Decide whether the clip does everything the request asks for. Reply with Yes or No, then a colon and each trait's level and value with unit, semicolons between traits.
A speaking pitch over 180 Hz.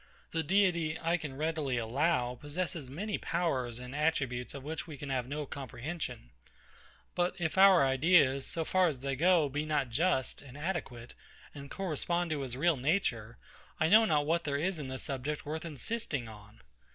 No: medium, 150 Hz